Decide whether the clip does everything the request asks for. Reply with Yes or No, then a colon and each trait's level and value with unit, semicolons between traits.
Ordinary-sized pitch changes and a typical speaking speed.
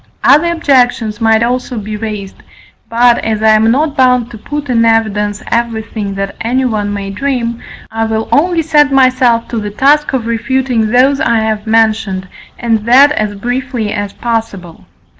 Yes: average, 3.1 semitones; average, 160 wpm